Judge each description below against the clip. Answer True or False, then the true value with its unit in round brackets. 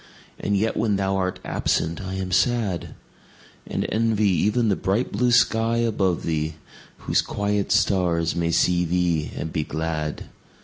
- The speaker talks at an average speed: True (150 wpm)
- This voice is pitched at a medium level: False (95 Hz)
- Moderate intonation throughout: True (4.2 semitones)